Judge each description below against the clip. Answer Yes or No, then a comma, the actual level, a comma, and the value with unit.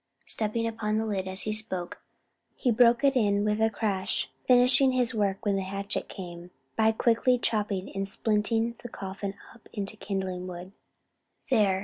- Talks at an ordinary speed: Yes, average, 165 wpm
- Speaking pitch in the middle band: No, high, 210 Hz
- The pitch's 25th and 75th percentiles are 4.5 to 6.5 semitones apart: No, average, 2.8 semitones